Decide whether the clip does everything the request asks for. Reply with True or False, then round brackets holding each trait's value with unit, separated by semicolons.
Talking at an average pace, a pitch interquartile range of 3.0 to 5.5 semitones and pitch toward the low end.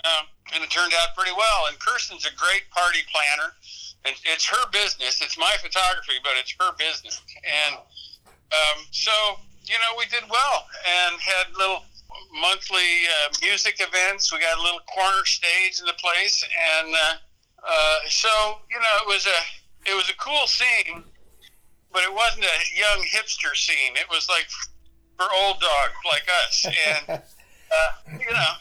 False (170 wpm; 4.9 semitones; 185 Hz)